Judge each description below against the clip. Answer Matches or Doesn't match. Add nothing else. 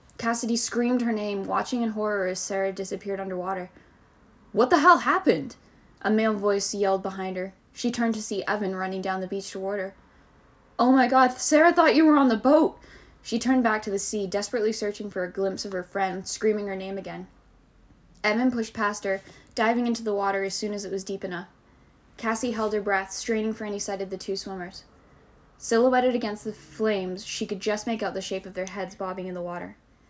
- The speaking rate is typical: Doesn't match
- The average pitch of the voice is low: Doesn't match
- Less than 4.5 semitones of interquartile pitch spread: Matches